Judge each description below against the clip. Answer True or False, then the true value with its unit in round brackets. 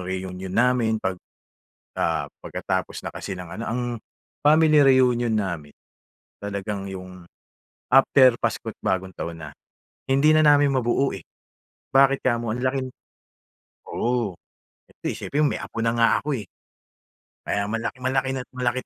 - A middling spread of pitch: False (5.7 semitones)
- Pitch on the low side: True (115 Hz)